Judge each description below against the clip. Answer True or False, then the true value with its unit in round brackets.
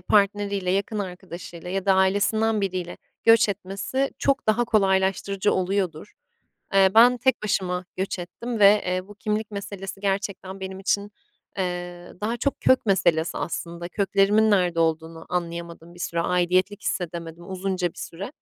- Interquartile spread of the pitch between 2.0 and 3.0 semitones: True (2.5 semitones)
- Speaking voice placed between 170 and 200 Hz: True (190 Hz)